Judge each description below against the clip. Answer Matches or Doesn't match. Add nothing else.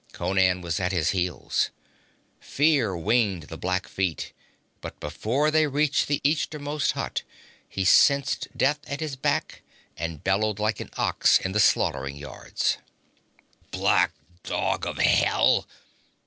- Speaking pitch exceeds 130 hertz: Doesn't match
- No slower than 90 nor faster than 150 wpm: Matches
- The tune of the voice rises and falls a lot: Matches